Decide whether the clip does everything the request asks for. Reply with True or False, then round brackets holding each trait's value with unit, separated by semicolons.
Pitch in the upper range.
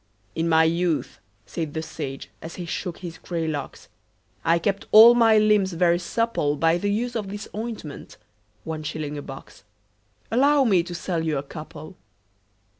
False (170 Hz)